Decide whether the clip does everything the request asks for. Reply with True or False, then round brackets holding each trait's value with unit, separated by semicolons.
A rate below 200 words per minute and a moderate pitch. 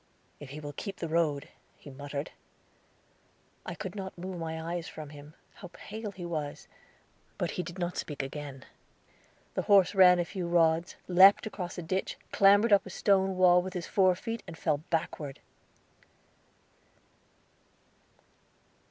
True (150 wpm; 175 Hz)